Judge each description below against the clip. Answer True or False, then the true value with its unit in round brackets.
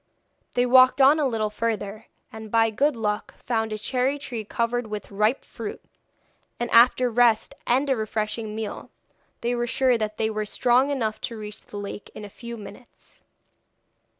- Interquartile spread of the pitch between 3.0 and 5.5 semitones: False (2.6 semitones)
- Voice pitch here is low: False (230 Hz)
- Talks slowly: False (180 wpm)